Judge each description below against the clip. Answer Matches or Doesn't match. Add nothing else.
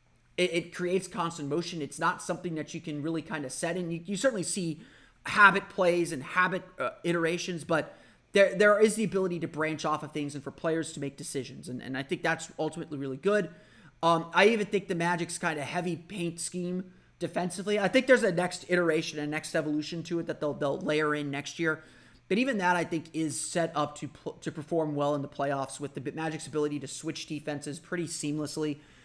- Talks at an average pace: Doesn't match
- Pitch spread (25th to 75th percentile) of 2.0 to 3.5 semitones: Matches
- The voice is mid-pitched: Matches